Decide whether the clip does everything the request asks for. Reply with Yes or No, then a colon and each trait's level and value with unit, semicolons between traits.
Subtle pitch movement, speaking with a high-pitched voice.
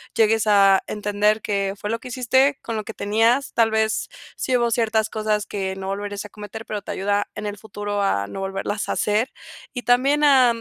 Yes: narrow, 2.2 semitones; high, 215 Hz